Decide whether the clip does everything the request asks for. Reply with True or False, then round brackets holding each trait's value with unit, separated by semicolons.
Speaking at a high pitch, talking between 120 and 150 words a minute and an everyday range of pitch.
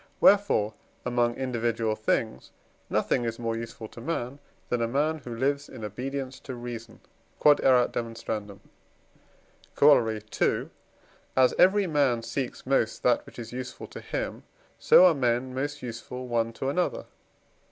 False (125 Hz; 140 wpm; 3.2 semitones)